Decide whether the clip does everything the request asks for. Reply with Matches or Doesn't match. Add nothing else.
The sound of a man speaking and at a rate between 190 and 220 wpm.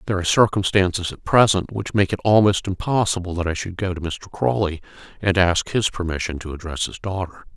Matches